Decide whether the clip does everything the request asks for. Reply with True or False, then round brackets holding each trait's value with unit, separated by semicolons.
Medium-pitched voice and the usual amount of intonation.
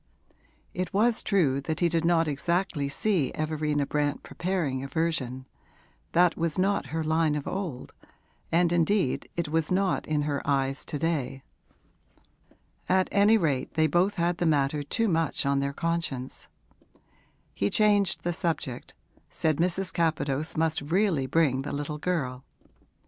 True (160 Hz; 3.6 semitones)